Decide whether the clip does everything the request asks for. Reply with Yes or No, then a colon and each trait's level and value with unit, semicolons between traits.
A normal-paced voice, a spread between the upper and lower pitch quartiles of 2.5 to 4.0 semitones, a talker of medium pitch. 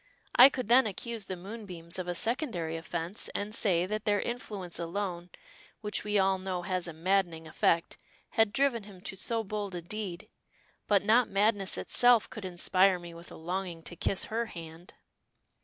No: average, 175 wpm; average, 3.6 semitones; high, 195 Hz